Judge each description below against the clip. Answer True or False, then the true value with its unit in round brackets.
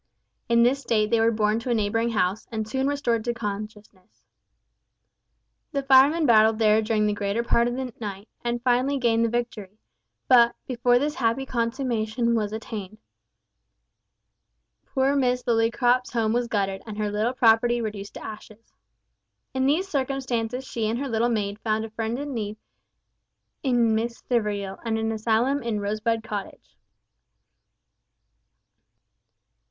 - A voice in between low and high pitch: False (230 Hz)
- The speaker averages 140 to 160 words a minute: True (145 wpm)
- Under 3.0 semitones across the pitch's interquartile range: True (2.4 semitones)